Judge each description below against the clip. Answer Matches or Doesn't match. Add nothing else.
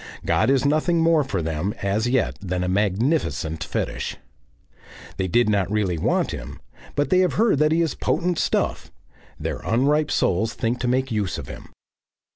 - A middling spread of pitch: Doesn't match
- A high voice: Doesn't match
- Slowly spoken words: Doesn't match